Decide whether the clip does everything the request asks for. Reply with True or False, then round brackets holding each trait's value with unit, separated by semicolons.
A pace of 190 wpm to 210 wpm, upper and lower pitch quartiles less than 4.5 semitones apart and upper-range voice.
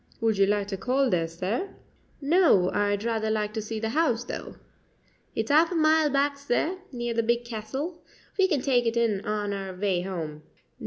False (200 wpm; 5.6 semitones; 230 Hz)